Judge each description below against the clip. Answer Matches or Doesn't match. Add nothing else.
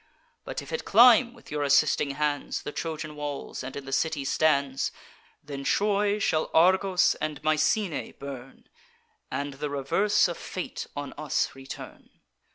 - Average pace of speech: Matches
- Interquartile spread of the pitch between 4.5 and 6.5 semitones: Matches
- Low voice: Doesn't match